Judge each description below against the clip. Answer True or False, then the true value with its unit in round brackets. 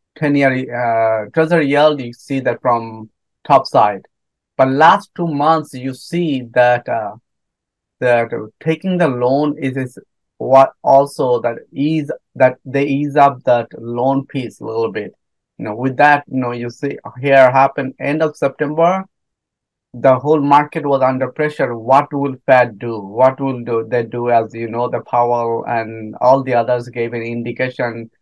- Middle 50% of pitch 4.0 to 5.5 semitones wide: False (3.2 semitones)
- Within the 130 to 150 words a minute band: False (165 wpm)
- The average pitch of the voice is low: True (130 Hz)